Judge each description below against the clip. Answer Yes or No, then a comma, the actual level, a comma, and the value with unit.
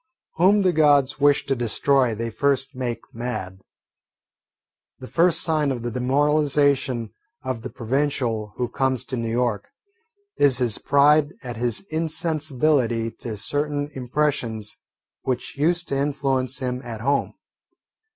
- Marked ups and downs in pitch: No, average, 3.5 semitones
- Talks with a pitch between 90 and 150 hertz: Yes, low, 135 Hz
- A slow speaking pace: Yes, slow, 130 wpm